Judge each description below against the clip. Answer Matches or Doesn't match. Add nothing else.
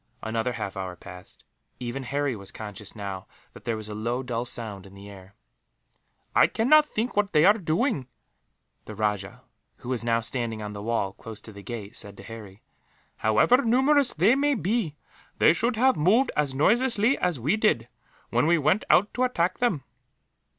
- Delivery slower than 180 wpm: Doesn't match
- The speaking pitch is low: Matches